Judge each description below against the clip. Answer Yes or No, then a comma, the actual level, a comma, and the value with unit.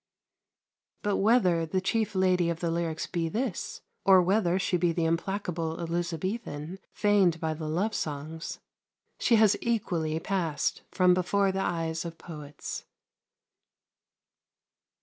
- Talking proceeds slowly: Yes, slow, 130 wpm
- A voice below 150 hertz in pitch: No, medium, 175 Hz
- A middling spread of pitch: Yes, average, 3.0 semitones